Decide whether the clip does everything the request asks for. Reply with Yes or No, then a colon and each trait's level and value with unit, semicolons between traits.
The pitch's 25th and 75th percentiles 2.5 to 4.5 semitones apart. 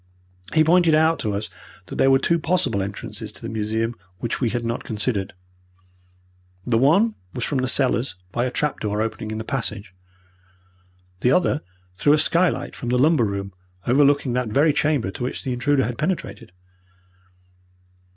No: average, 5.2 semitones